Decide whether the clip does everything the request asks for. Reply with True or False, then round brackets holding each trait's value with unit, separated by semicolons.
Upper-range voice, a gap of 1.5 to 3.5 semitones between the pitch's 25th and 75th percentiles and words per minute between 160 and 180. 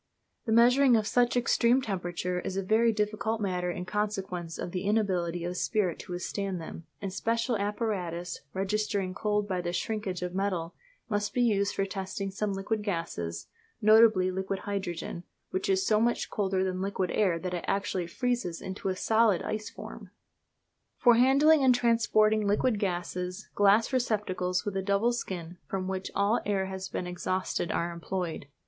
True (195 Hz; 3.0 semitones; 170 wpm)